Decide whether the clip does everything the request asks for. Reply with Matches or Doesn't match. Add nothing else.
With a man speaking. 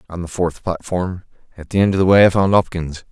Matches